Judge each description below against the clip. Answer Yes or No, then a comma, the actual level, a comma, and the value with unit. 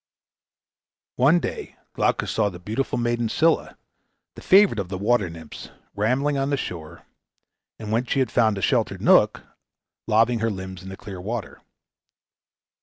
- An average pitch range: Yes, average, 4.7 semitones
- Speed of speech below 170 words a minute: Yes, average, 155 wpm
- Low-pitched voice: Yes, low, 110 Hz